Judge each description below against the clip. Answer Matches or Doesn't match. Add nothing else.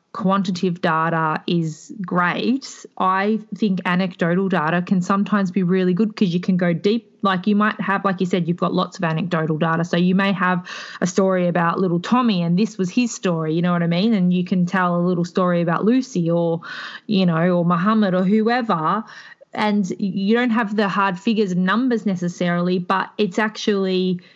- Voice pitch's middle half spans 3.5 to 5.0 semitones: Doesn't match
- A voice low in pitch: Doesn't match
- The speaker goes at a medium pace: Matches